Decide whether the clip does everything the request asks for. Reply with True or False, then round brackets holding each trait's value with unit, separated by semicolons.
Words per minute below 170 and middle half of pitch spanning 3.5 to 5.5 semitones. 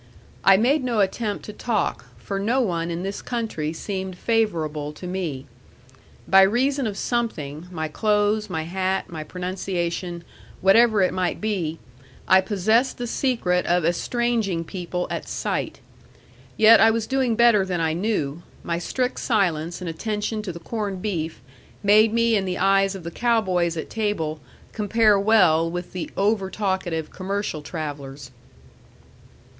True (150 wpm; 4.3 semitones)